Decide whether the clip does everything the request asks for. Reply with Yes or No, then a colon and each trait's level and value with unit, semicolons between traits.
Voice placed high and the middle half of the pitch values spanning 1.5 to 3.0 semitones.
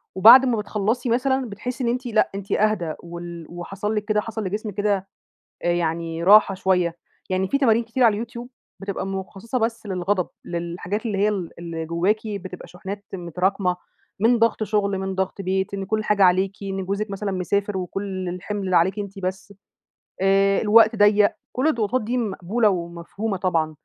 Yes: high, 200 Hz; average, 2.7 semitones